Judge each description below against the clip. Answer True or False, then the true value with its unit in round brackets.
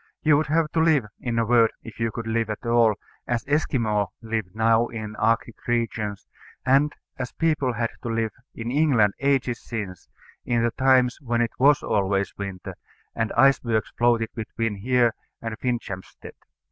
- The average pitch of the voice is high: False (115 Hz)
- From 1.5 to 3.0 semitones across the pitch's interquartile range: True (2.5 semitones)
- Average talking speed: True (165 wpm)